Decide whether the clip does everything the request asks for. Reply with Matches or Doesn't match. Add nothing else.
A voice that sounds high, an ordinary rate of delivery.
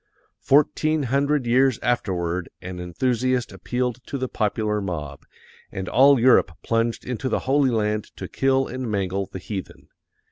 Doesn't match